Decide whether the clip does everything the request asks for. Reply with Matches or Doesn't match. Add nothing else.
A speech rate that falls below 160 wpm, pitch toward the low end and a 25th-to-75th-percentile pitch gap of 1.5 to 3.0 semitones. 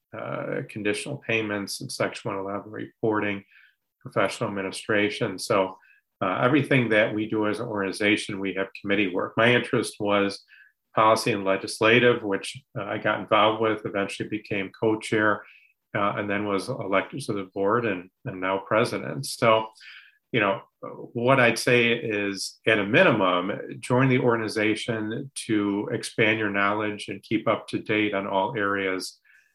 Matches